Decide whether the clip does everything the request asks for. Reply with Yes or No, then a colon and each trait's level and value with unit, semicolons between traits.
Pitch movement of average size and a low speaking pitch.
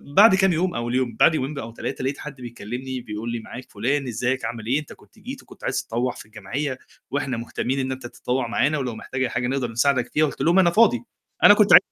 Yes: average, 3.1 semitones; low, 130 Hz